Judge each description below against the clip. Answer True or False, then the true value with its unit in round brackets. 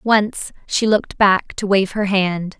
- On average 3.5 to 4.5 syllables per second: True (3.7 syllables/s)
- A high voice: True (200 Hz)